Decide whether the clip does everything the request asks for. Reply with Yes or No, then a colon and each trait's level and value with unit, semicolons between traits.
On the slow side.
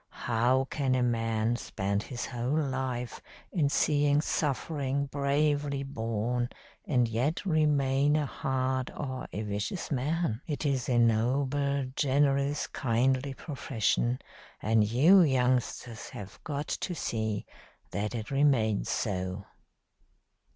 Yes: slow, 115 wpm